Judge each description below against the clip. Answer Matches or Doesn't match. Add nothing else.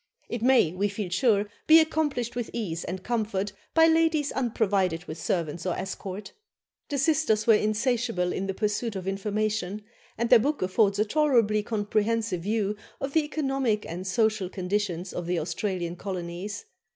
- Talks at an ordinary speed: Matches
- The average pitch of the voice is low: Doesn't match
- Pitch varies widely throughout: Doesn't match